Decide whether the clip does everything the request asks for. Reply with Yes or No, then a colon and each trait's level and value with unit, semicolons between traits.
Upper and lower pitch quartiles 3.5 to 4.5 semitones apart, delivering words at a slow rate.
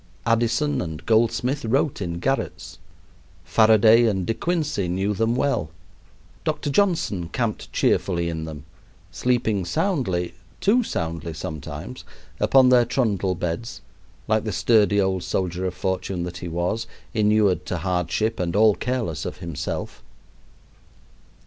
No: average, 5.1 semitones; slow, 130 wpm